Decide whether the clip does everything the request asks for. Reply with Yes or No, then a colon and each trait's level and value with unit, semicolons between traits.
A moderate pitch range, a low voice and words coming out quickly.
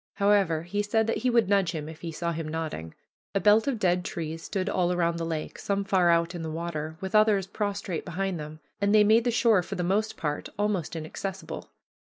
No: average, 3.9 semitones; medium, 185 Hz; fast, 225 wpm